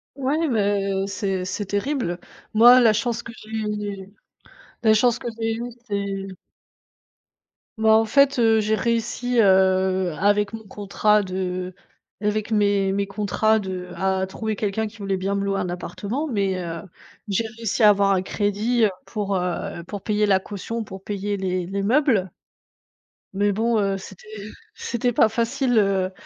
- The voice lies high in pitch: Yes, high, 205 Hz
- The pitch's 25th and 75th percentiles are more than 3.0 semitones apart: No, narrow, 2.5 semitones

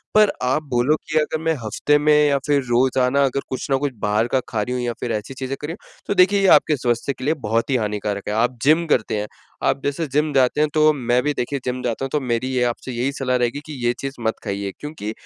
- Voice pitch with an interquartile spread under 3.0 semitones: No, average, 3.6 semitones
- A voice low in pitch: Yes, low, 130 Hz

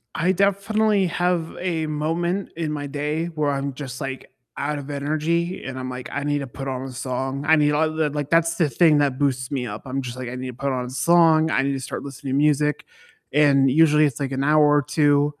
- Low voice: No, medium, 145 Hz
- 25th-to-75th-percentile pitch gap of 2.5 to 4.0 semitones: Yes, average, 2.9 semitones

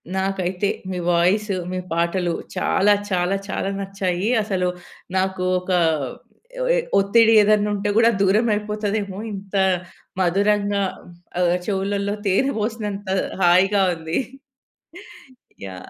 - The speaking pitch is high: Yes, high, 195 Hz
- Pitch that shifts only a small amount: Yes, narrow, 2.1 semitones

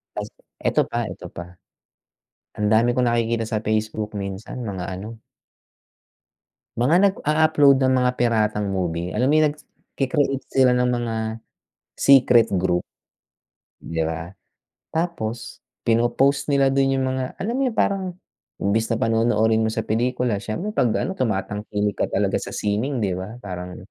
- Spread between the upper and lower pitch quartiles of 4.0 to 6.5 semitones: Yes, average, 4.3 semitones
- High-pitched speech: No, low, 115 Hz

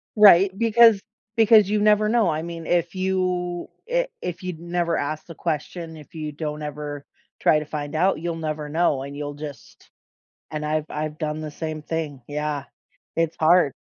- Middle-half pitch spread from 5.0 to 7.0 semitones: No, average, 3.1 semitones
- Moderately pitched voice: Yes, medium, 160 Hz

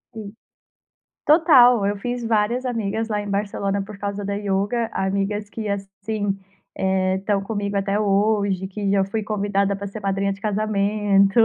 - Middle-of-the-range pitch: No, high, 200 Hz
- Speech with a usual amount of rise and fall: No, narrow, 1.4 semitones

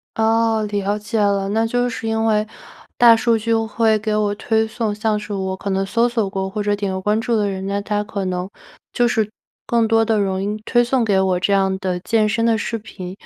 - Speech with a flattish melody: Yes, narrow, 2.2 semitones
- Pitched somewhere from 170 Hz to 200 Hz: No, high, 210 Hz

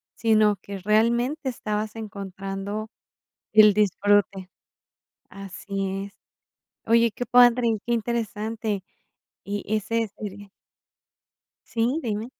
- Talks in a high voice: Yes, high, 215 Hz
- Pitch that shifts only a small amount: Yes, narrow, 2.3 semitones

